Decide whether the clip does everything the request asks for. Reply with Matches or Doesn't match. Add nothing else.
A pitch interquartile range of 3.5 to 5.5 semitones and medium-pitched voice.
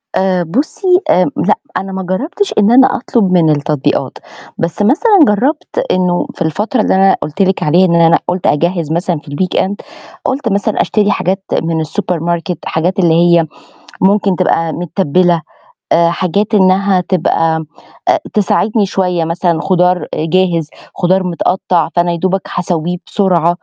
Doesn't match